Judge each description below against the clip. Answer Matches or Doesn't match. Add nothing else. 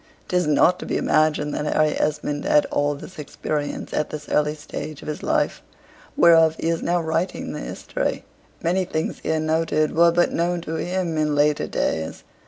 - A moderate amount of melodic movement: Doesn't match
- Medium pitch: Matches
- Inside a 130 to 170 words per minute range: Doesn't match